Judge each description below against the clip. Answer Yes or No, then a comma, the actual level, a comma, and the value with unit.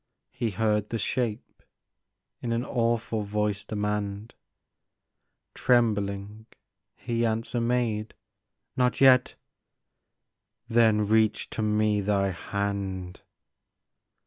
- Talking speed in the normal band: No, slow, 105 wpm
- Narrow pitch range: Yes, narrow, 2.3 semitones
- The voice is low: Yes, low, 110 Hz